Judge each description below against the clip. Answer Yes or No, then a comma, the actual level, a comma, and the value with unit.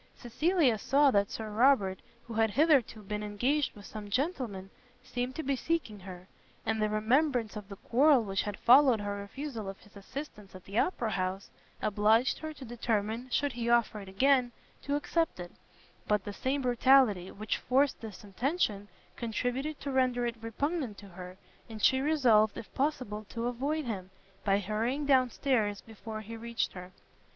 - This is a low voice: No, high, 230 Hz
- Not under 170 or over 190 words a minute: Yes, average, 175 wpm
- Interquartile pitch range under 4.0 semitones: No, average, 4.5 semitones